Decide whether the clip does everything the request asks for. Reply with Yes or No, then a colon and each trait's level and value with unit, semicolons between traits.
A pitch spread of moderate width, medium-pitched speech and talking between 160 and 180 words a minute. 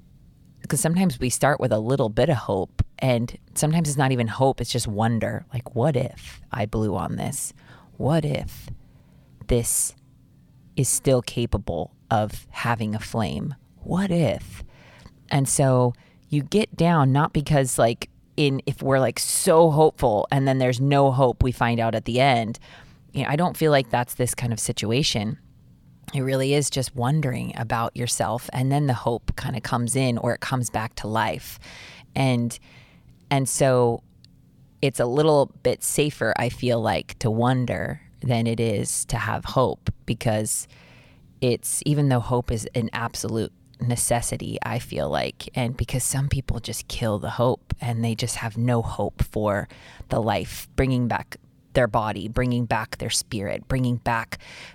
No: average, 3.0 semitones; low, 125 Hz; average, 170 wpm